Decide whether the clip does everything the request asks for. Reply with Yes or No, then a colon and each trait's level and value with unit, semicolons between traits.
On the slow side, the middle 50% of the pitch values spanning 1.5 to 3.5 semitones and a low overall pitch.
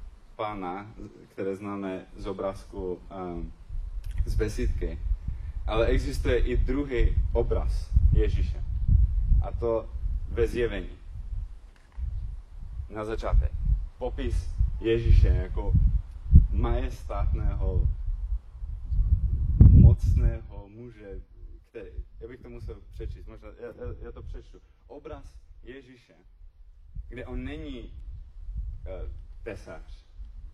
No: slow, 85 wpm; average, 4.1 semitones; very low, 85 Hz